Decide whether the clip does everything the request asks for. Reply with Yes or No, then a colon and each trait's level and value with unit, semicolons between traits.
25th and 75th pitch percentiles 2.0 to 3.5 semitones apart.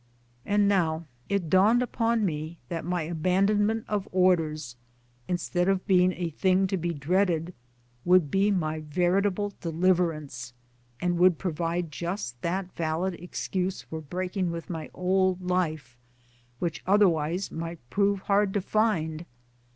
Yes: average, 3.0 semitones